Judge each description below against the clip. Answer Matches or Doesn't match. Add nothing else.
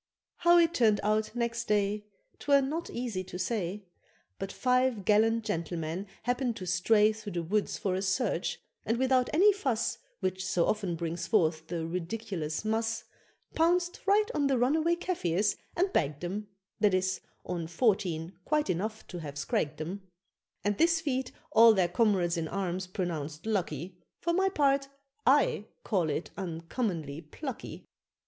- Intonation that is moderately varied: Doesn't match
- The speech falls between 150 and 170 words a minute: Matches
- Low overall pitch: Doesn't match